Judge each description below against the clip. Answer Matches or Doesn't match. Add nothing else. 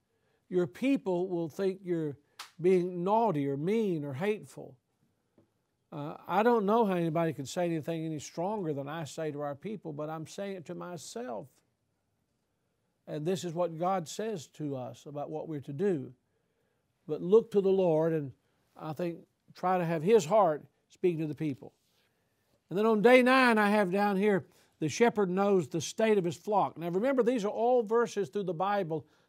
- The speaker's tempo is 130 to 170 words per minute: Doesn't match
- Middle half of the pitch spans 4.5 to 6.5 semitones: Matches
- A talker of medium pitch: Matches